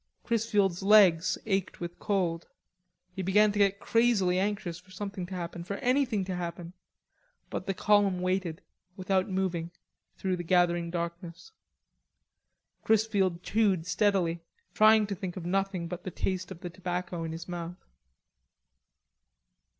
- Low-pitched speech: No, medium, 185 Hz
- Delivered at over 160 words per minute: No, average, 140 wpm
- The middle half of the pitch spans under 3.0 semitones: Yes, narrow, 2.6 semitones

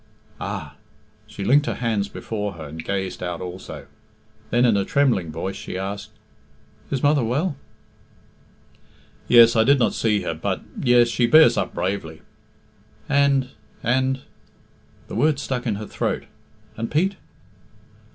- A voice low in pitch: Yes, low, 115 Hz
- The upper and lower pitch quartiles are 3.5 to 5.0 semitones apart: No, wide, 5.5 semitones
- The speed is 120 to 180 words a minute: Yes, average, 145 wpm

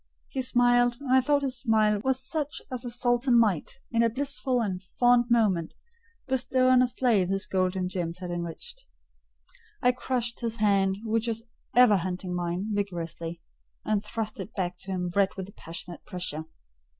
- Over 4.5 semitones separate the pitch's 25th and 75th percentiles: Yes, average, 5.0 semitones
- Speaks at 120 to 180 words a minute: Yes, average, 175 wpm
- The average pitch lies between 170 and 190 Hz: No, high, 220 Hz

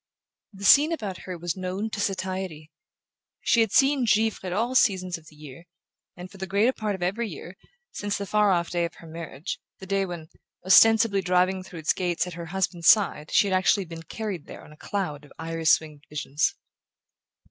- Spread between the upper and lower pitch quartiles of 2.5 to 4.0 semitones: Yes, average, 3.4 semitones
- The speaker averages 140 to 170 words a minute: No, average, 200 wpm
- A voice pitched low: No, medium, 185 Hz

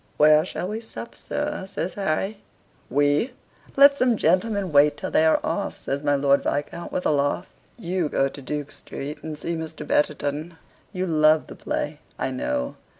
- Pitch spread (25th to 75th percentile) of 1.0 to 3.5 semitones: No, average, 4.3 semitones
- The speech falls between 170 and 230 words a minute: Yes, average, 175 wpm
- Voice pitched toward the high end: No, medium, 155 Hz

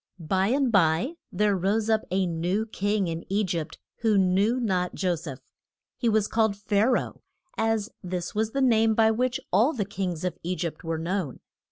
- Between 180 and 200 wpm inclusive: Yes, average, 195 wpm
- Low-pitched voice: No, high, 200 Hz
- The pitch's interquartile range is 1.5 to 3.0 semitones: No, average, 3.7 semitones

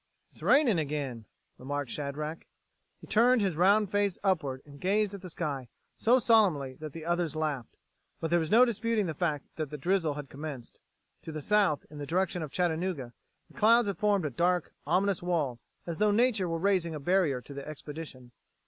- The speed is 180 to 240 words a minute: Yes, average, 190 wpm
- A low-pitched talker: No, medium, 165 Hz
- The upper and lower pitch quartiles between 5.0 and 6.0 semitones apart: Yes, average, 5.3 semitones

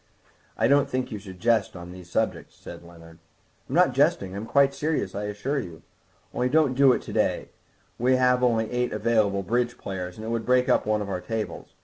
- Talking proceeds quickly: Yes, fast, 215 wpm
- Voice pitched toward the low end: Yes, low, 110 Hz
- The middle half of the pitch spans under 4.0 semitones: No, average, 4.4 semitones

